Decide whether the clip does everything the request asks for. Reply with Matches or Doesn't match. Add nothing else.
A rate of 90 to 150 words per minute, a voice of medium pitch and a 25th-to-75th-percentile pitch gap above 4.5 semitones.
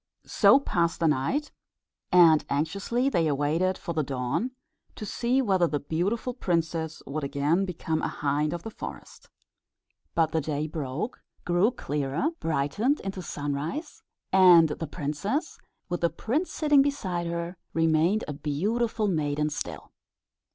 Matches